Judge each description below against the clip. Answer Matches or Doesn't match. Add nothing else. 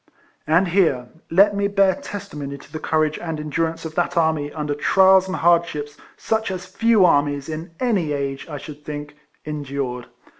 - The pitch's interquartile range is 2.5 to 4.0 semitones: Doesn't match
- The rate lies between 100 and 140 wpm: Doesn't match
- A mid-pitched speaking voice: Matches